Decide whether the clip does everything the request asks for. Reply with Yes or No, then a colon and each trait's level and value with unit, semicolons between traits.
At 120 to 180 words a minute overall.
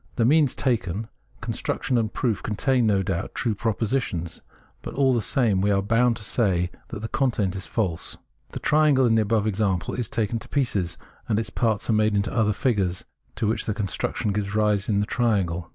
No: average, 195 wpm